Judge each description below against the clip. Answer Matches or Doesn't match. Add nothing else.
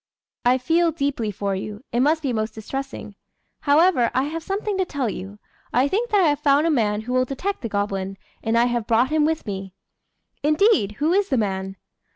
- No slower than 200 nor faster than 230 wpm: Matches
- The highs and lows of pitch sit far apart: Matches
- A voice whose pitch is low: Doesn't match